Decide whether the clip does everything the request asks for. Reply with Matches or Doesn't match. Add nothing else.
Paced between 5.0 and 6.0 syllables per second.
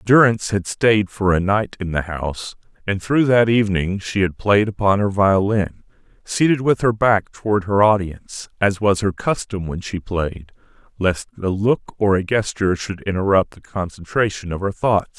Doesn't match